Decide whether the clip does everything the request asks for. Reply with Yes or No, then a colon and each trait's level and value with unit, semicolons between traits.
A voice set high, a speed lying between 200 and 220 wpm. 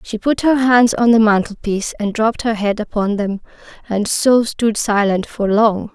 No: high, 215 Hz; average, 190 wpm